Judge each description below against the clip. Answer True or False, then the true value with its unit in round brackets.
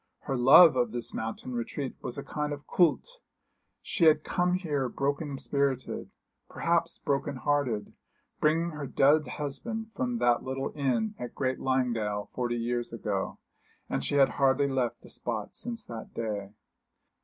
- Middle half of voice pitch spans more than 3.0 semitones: True (3.7 semitones)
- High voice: False (135 Hz)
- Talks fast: False (155 wpm)